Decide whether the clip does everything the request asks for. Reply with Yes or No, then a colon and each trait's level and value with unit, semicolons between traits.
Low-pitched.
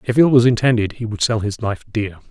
Yes: low, 115 Hz